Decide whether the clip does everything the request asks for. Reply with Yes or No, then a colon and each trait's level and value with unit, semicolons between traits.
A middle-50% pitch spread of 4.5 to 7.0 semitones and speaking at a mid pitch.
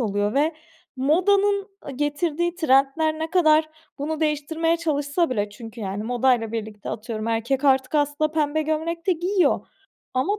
No: average, 4.9 semitones; very high, 295 Hz